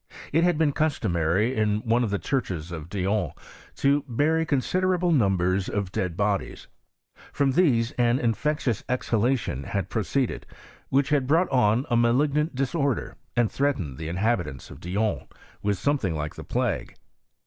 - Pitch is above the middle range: No, low, 115 Hz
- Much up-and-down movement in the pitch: Yes, wide, 6.5 semitones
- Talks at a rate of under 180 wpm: Yes, average, 150 wpm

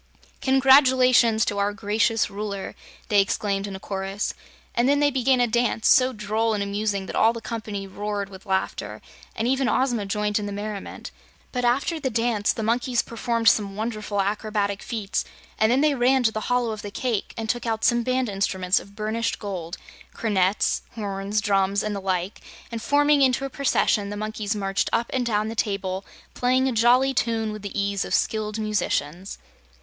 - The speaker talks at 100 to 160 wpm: No, average, 185 wpm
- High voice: Yes, high, 215 Hz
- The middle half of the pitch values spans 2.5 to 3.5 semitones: Yes, average, 3.2 semitones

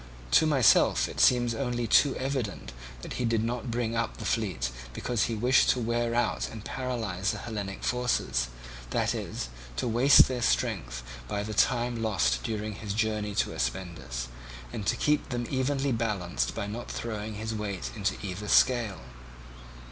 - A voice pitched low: Yes, low, 110 Hz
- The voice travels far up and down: No, average, 3.3 semitones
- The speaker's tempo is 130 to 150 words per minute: No, average, 165 wpm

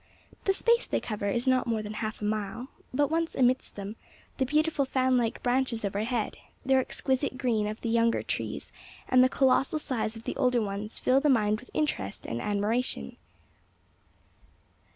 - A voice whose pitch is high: Yes, high, 245 Hz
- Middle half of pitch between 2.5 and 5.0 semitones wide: Yes, average, 3.6 semitones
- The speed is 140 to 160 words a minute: No, average, 175 wpm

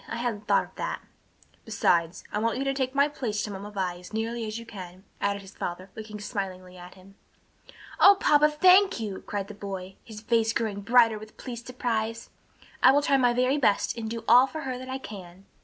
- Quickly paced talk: Yes, fast, 215 wpm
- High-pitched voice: Yes, high, 220 Hz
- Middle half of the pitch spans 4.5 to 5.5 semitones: No, average, 4.1 semitones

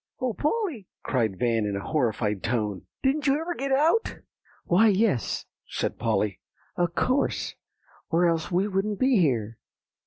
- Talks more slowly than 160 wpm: Yes, average, 150 wpm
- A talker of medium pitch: Yes, medium, 175 Hz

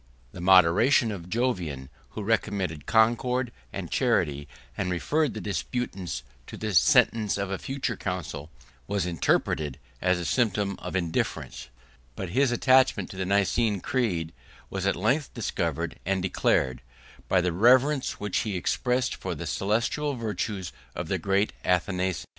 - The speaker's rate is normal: Yes, average, 150 wpm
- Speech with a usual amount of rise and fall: Yes, average, 4.9 semitones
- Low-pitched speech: Yes, low, 100 Hz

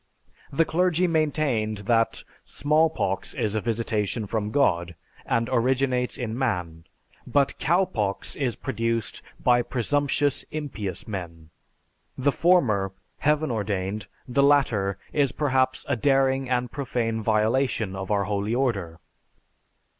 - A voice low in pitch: Yes, low, 120 Hz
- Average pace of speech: No, slow, 115 wpm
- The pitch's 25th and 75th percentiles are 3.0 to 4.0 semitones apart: No, average, 5.0 semitones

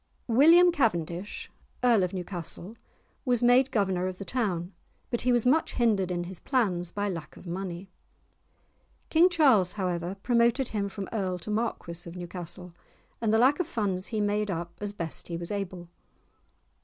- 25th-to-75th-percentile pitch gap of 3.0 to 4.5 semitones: No, average, 5.0 semitones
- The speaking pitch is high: Yes, high, 200 Hz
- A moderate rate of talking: Yes, average, 170 wpm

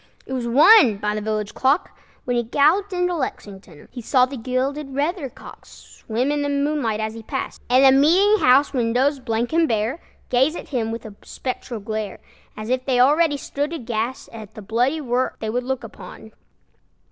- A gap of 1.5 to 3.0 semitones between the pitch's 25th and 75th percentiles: No, average, 4.3 semitones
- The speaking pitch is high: Yes, very high, 255 Hz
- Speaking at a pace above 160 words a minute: Yes, average, 185 wpm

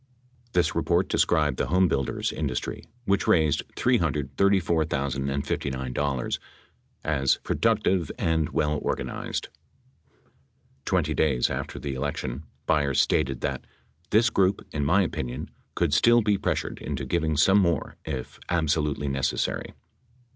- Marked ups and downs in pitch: No, average, 4.2 semitones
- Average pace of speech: No, slow, 120 wpm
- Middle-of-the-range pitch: No, very low, 75 Hz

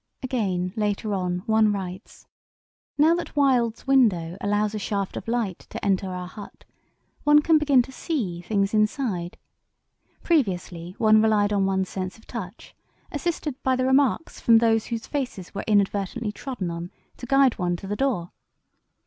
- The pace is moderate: Yes, average, 160 wpm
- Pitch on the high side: Yes, high, 215 Hz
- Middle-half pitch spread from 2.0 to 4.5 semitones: No, average, 5.2 semitones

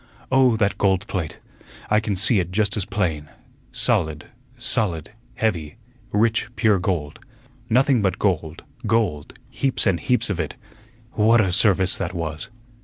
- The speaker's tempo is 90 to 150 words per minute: Yes, average, 145 wpm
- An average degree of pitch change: Yes, average, 4.5 semitones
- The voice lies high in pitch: No, low, 100 Hz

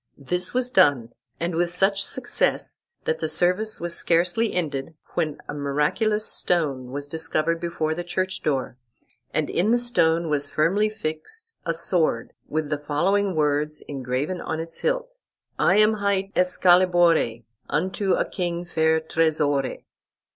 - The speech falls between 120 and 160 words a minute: Yes, average, 145 wpm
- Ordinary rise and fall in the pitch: Yes, average, 3.8 semitones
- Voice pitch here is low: No, medium, 170 Hz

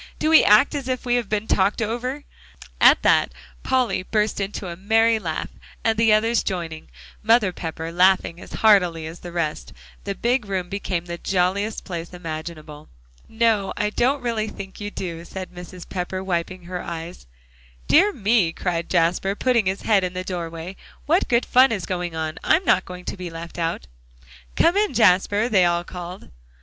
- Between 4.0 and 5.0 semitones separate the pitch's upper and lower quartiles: Yes, average, 4.4 semitones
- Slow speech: No, average, 180 wpm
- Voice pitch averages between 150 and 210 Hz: Yes, high, 190 Hz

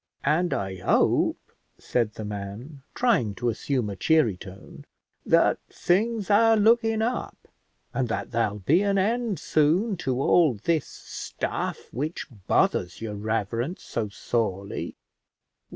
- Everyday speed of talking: No, slow, 130 wpm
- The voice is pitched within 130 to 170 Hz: Yes, low, 135 Hz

